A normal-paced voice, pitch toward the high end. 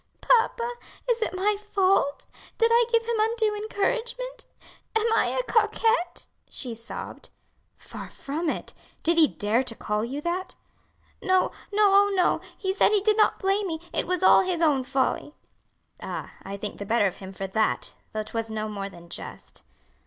Yes: average, 175 wpm; very high, 370 Hz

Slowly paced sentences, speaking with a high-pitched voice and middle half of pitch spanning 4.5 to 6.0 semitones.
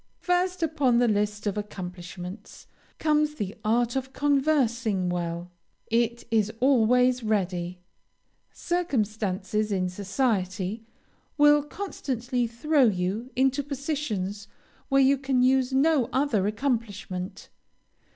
Yes: slow, 105 wpm; high, 235 Hz; average, 5.3 semitones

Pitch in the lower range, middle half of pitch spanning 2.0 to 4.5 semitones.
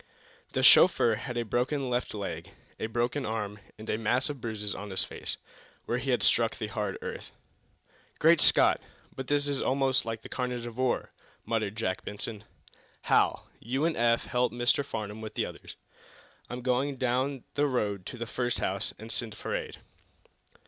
Yes: low, 120 Hz; average, 3.1 semitones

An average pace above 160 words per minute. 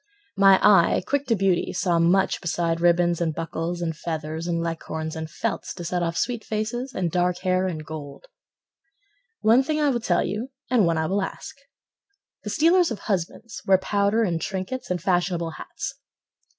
Yes: average, 175 wpm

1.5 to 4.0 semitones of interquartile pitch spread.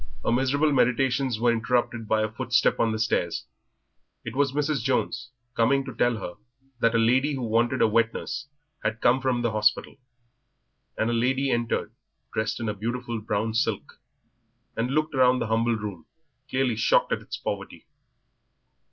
Yes: average, 2.8 semitones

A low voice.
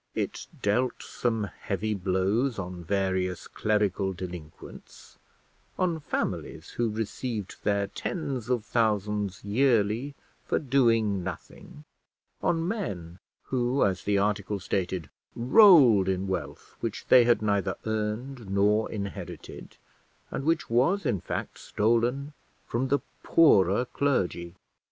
Yes: low, 105 Hz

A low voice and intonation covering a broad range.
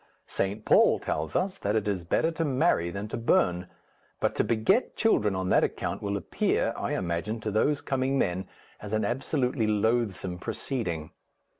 Yes: low, 110 Hz; wide, 5.8 semitones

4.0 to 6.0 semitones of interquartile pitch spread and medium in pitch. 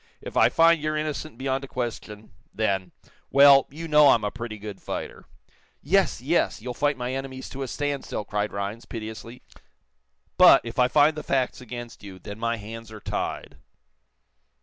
No: average, 4.4 semitones; low, 125 Hz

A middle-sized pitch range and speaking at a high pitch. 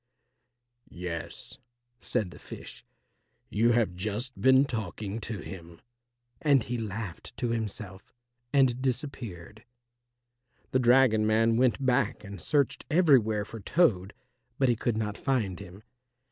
No: average, 4.1 semitones; low, 115 Hz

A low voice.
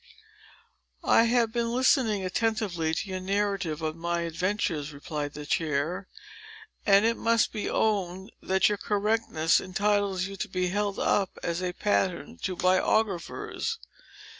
No: high, 190 Hz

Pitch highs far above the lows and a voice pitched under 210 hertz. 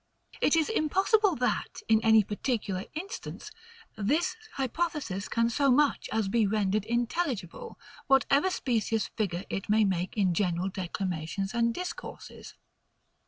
No: wide, 6.5 semitones; high, 225 Hz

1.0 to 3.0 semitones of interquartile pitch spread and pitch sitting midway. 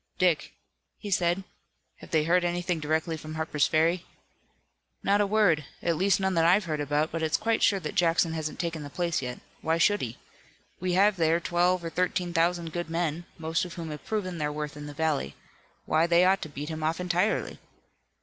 Yes: narrow, 2.4 semitones; medium, 170 Hz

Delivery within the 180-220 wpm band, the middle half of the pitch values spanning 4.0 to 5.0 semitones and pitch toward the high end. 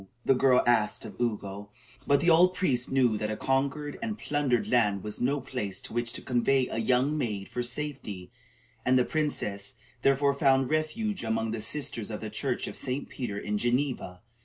No: average, 185 wpm; average, 4.6 semitones; low, 125 Hz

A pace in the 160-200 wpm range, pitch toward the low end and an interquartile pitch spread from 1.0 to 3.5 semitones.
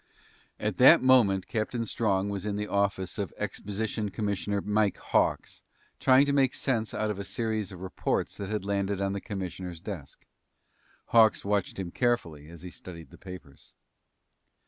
Yes: average, 165 wpm; low, 100 Hz; narrow, 2.5 semitones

